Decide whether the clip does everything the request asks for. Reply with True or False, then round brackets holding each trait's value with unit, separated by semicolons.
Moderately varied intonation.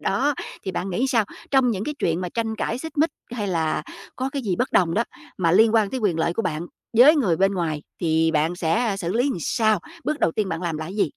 False (6.0 semitones)